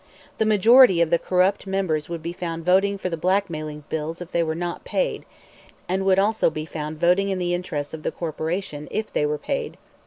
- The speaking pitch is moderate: Yes, medium, 175 Hz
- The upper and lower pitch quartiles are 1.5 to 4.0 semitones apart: Yes, average, 3.5 semitones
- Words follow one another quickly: Yes, fast, 210 wpm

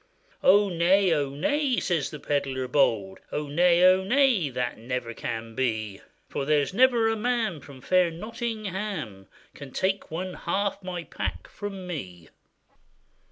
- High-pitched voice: No, medium, 170 Hz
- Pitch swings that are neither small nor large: No, wide, 7.0 semitones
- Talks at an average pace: Yes, average, 145 wpm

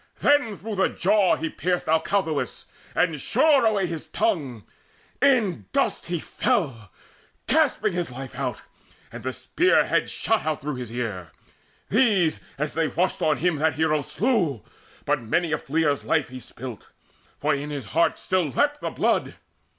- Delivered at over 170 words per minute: No, average, 160 wpm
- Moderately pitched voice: Yes, medium, 160 Hz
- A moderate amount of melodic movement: No, wide, 6.3 semitones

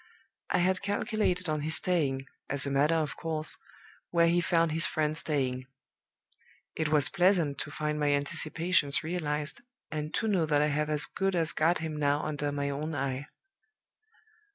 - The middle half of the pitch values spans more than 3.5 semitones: No, narrow, 2.5 semitones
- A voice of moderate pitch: Yes, medium, 155 Hz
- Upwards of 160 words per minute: Yes, average, 170 wpm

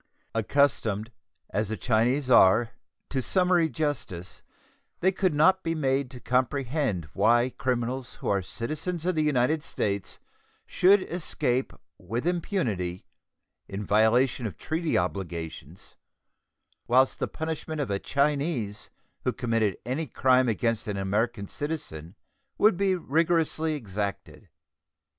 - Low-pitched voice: Yes, low, 125 Hz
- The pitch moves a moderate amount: No, wide, 6.7 semitones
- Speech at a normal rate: No, slow, 125 wpm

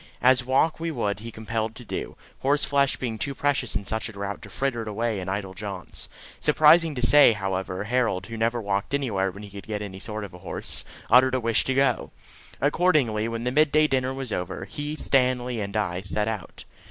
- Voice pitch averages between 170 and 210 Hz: No, low, 115 Hz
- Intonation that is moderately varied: Yes, average, 4.6 semitones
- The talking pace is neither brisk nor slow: No, fast, 210 wpm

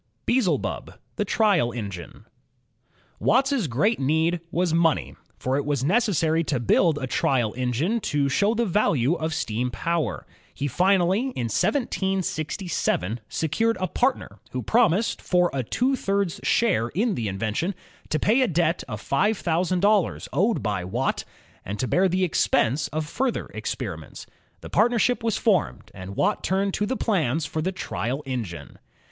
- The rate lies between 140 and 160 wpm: Yes, average, 155 wpm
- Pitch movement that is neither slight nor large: No, wide, 7.7 semitones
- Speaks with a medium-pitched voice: Yes, medium, 170 Hz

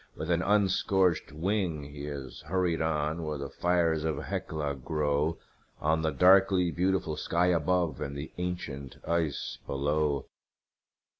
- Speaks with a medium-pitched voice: No, very low, 80 Hz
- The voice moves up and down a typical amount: Yes, average, 3.4 semitones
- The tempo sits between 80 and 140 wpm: Yes, slow, 135 wpm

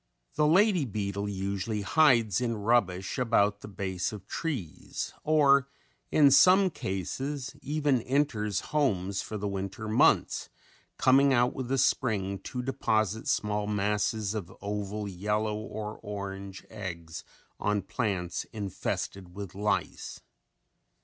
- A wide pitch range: No, average, 4.6 semitones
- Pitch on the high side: No, low, 105 Hz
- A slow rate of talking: Yes, slow, 125 wpm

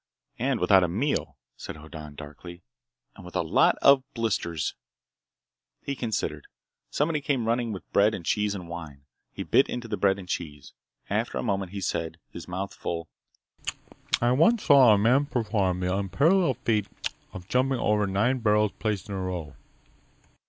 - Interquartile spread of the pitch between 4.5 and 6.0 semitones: Yes, average, 5.3 semitones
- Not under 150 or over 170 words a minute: Yes, average, 165 wpm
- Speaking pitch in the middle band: No, low, 100 Hz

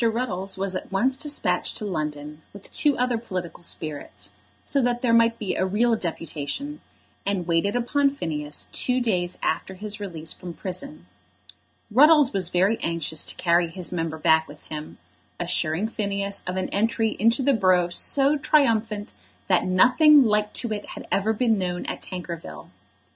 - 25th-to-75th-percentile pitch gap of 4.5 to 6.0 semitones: Yes, wide, 5.4 semitones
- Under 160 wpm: No, average, 165 wpm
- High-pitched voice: Yes, high, 200 Hz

